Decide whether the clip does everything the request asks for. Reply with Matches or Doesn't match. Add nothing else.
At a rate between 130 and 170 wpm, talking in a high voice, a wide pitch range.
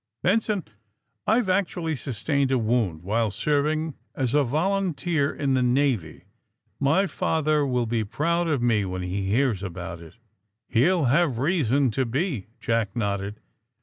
Doesn't match